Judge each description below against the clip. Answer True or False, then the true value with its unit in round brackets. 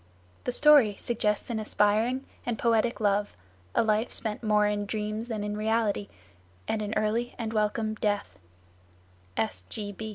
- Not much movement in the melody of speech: True (1.7 semitones)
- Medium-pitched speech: False (215 Hz)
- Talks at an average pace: False (130 wpm)